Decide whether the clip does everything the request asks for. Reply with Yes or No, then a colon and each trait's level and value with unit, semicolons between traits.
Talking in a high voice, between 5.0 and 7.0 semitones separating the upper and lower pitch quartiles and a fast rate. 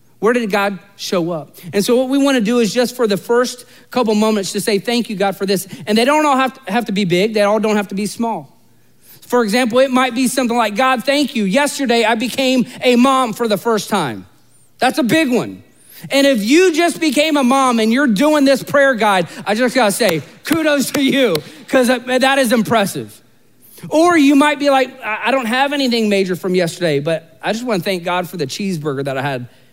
Yes: high, 230 Hz; wide, 5.4 semitones; fast, 235 wpm